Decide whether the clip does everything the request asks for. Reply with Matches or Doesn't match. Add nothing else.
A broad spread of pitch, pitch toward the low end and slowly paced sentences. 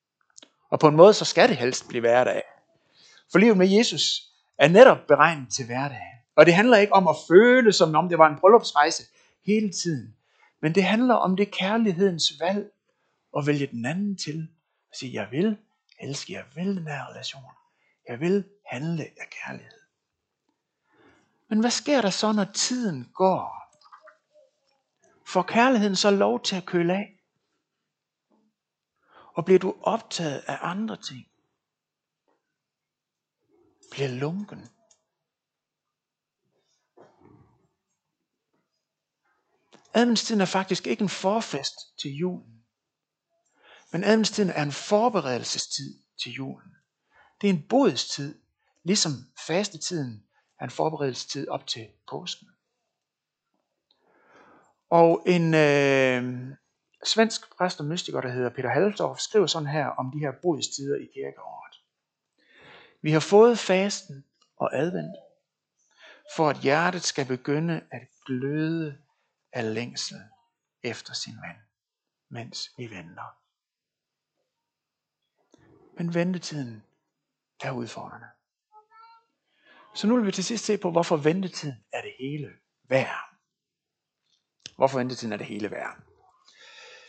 Doesn't match